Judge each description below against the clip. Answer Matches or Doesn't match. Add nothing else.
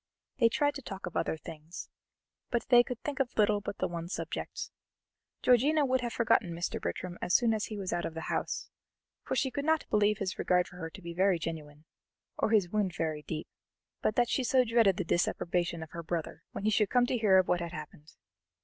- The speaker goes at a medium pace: Doesn't match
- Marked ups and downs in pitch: Matches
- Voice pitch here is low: Doesn't match